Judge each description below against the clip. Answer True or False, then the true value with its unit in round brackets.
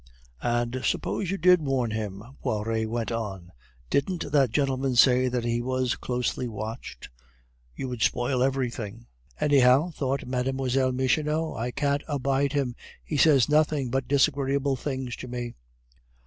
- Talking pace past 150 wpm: False (140 wpm)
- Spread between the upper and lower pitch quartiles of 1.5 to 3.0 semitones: True (2.7 semitones)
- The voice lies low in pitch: True (130 Hz)